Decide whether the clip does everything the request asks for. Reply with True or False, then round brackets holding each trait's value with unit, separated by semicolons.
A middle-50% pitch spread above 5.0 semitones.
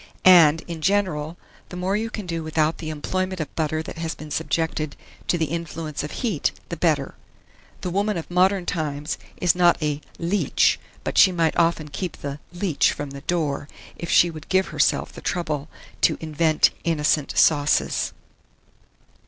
False (2.7 semitones)